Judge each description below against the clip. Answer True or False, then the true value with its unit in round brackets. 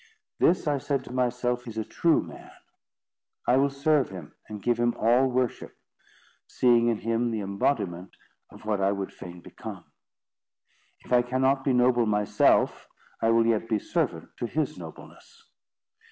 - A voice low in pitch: True (120 Hz)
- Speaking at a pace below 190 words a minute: True (160 wpm)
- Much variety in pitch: False (3.4 semitones)